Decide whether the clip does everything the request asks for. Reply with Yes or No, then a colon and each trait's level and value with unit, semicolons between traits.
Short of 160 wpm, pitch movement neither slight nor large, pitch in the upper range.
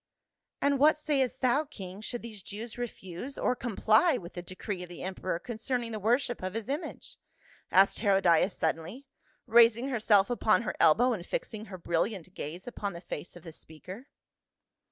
No: average, 175 wpm; average, 4.9 semitones; high, 215 Hz